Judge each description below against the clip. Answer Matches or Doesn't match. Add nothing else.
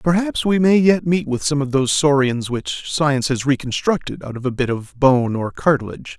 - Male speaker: Matches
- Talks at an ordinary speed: Doesn't match